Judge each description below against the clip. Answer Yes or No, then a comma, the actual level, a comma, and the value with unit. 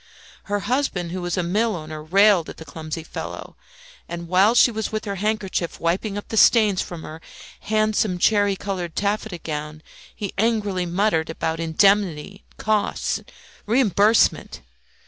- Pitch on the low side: No, high, 195 Hz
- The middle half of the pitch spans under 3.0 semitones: No, average, 4.0 semitones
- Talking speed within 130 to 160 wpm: Yes, average, 145 wpm